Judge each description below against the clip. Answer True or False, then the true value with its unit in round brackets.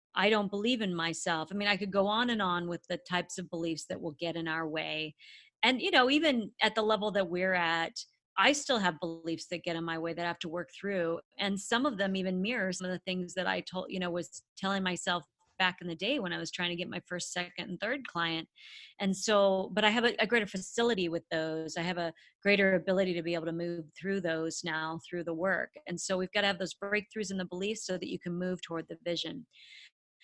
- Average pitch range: True (3.0 semitones)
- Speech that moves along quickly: True (255 wpm)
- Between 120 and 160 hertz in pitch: False (180 Hz)